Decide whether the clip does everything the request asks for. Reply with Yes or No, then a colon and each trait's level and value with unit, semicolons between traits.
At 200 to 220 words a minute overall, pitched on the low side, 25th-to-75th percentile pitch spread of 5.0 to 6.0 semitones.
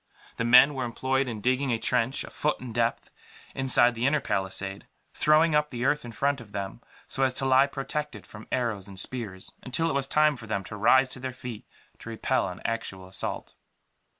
No: fast, 205 wpm; low, 125 Hz; average, 3.5 semitones